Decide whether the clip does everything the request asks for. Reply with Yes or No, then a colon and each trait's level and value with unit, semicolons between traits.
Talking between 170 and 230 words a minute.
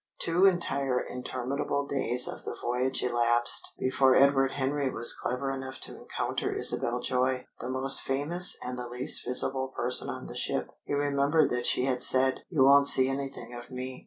Yes: average, 175 wpm